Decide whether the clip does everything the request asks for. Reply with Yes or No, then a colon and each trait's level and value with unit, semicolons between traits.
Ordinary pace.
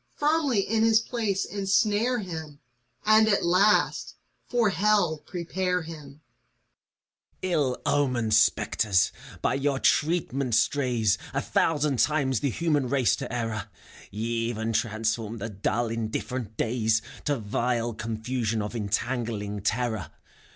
No: slow, 125 wpm